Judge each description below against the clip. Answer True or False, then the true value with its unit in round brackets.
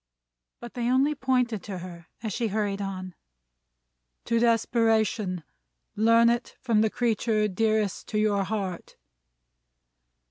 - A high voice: True (220 Hz)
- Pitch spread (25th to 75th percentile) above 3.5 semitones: False (2.8 semitones)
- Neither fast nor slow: False (120 wpm)